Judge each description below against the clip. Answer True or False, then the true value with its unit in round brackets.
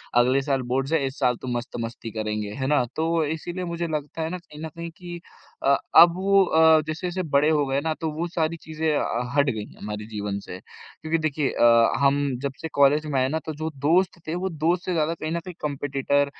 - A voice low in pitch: False (150 Hz)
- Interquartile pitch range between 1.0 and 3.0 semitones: False (3.5 semitones)